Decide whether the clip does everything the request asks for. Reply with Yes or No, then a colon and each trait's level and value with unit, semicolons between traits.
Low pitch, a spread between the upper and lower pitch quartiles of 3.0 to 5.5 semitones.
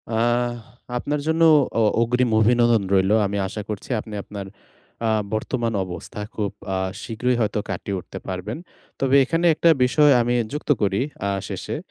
Yes: low, 115 Hz; average, 3.6 semitones